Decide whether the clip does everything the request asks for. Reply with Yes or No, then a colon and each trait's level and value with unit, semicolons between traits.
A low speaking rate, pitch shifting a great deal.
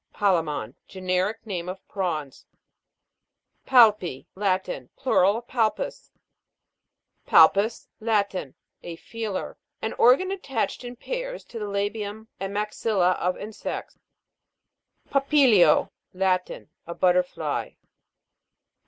No: slow, 100 wpm; average, 3.8 semitones